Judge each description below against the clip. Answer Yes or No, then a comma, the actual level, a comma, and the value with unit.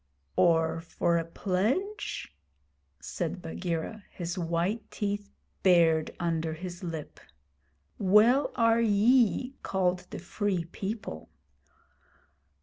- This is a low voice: No, medium, 185 Hz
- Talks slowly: Yes, slow, 95 wpm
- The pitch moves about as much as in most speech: Yes, average, 4.3 semitones